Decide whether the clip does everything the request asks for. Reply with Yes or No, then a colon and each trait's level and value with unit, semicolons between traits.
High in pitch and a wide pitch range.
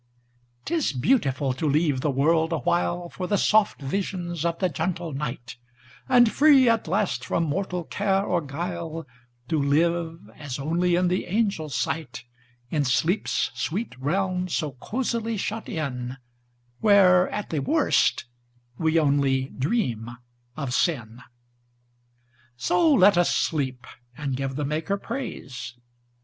No: medium, 155 Hz; wide, 6.0 semitones